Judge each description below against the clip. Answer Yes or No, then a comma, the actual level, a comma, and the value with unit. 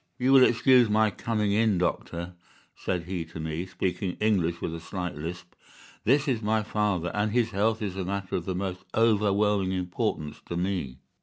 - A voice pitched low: Yes, very low, 95 Hz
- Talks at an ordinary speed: Yes, average, 180 wpm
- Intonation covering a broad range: No, average, 3.5 semitones